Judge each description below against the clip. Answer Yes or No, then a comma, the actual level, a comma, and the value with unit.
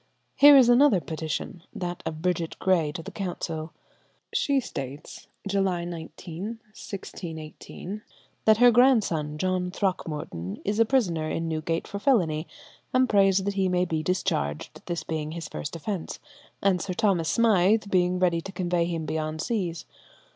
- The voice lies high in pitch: No, medium, 180 Hz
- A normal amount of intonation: Yes, average, 3.9 semitones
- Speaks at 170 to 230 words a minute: No, average, 150 wpm